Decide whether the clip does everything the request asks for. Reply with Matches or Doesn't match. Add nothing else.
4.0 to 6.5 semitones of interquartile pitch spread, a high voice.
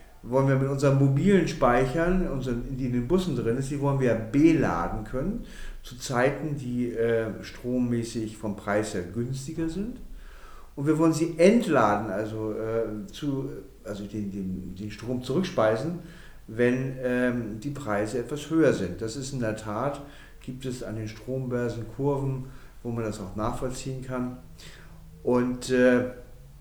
Doesn't match